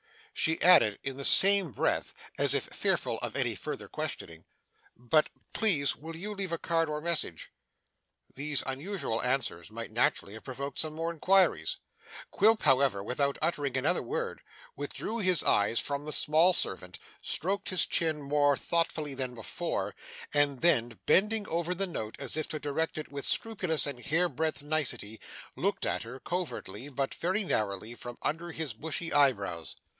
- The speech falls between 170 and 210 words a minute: No, average, 160 wpm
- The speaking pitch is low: No, medium, 150 Hz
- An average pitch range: Yes, average, 5.0 semitones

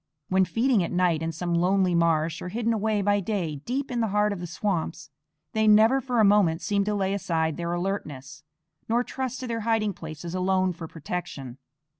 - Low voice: No, high, 190 Hz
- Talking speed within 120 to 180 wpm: No, average, 200 wpm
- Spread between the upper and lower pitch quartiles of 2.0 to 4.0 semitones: No, average, 4.4 semitones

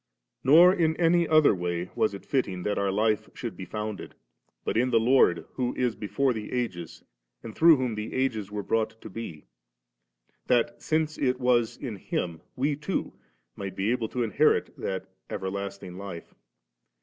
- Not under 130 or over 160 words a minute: No, average, 175 wpm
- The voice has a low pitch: Yes, low, 115 Hz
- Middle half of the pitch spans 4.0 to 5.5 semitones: Yes, average, 4.7 semitones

